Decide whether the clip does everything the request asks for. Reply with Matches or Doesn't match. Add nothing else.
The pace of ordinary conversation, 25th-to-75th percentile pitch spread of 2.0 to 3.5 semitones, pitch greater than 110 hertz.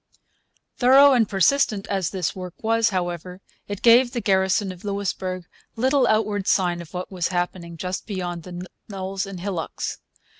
Matches